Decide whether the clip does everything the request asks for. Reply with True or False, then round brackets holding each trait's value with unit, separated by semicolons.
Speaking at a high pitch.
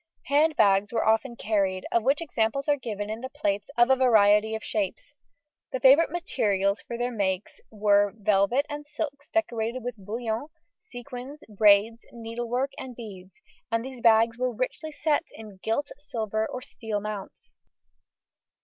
True (230 Hz)